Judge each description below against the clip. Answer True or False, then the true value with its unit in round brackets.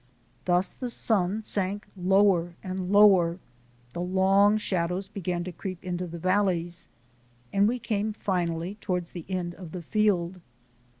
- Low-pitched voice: False (185 Hz)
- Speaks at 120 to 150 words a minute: True (140 wpm)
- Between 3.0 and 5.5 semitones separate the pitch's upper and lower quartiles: False (2.5 semitones)